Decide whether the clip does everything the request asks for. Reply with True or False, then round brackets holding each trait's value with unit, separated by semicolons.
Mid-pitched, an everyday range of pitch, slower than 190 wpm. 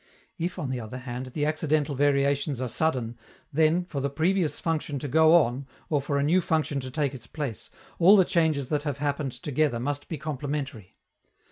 False (145 Hz; 3.1 semitones; 195 wpm)